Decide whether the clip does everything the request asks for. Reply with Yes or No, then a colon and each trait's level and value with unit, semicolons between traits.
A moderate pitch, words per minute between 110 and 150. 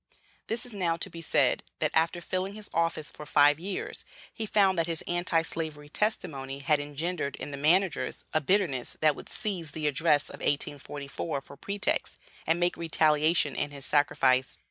No: medium, 160 Hz; average, 175 wpm